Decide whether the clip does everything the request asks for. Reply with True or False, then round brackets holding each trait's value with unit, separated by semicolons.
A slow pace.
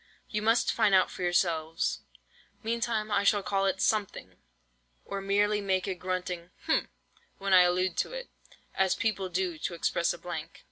False (155 wpm)